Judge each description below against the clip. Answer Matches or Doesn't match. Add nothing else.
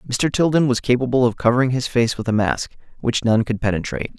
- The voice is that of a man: Matches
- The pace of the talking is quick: Matches